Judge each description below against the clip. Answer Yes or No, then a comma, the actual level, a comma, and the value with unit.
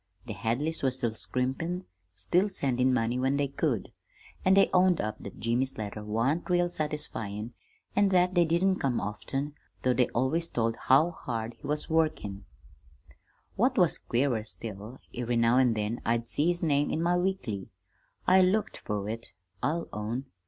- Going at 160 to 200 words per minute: Yes, average, 165 wpm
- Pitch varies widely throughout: Yes, wide, 6.4 semitones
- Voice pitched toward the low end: Yes, low, 130 Hz